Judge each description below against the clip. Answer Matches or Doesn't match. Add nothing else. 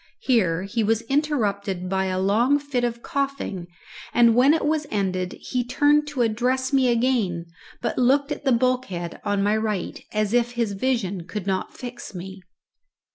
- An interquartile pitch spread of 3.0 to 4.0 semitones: Doesn't match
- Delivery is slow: Doesn't match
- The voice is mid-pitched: Doesn't match